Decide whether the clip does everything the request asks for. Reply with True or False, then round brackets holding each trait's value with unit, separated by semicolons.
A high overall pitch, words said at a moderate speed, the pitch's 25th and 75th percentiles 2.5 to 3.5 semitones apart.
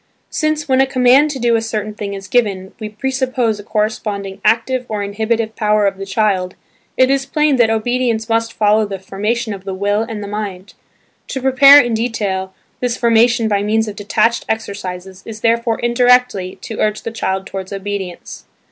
True (220 Hz; 185 wpm; 3.1 semitones)